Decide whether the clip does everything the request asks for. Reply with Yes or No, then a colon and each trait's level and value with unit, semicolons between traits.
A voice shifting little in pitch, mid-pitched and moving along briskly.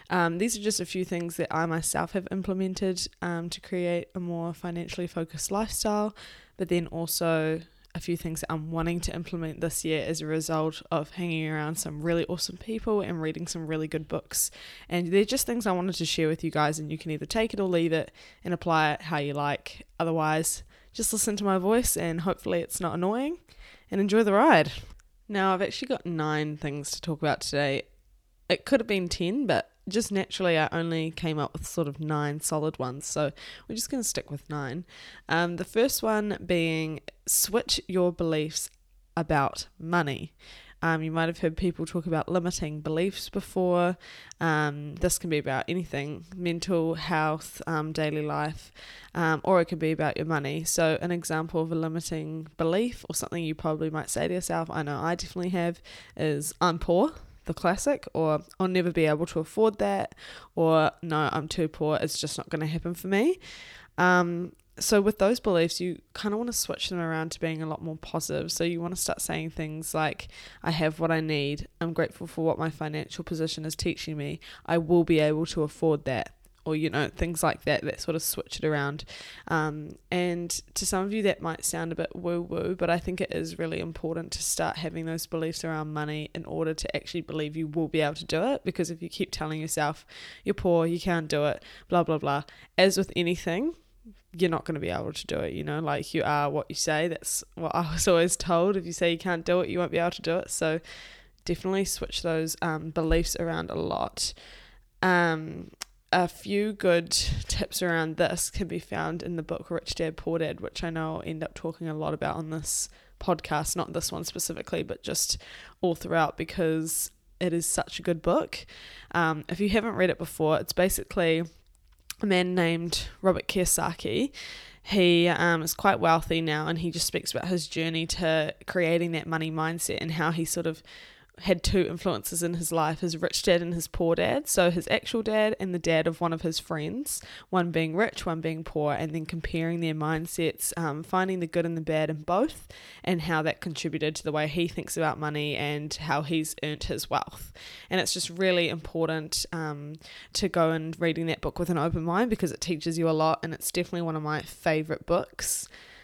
Yes: narrow, 2.1 semitones; medium, 165 Hz; fast, 210 wpm